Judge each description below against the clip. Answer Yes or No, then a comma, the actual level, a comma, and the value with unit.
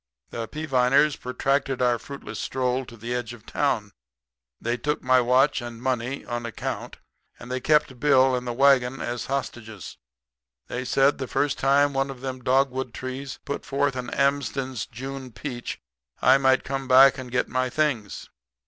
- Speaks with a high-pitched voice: No, low, 130 Hz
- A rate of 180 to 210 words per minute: No, average, 165 wpm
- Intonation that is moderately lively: No, narrow, 1.9 semitones